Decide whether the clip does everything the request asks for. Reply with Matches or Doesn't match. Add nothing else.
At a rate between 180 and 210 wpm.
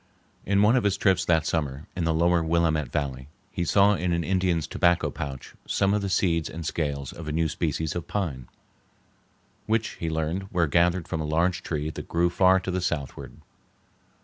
Matches